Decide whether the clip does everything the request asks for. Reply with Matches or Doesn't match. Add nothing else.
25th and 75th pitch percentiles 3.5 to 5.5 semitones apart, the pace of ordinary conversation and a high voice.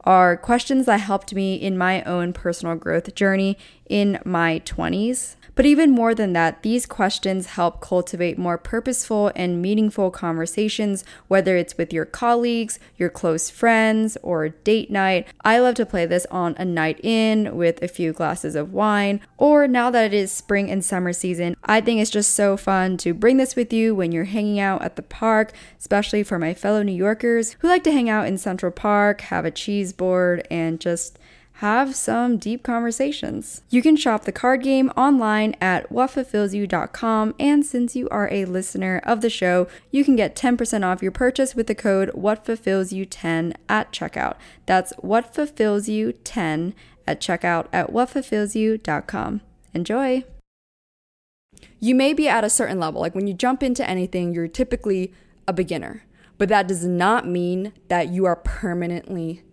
Matches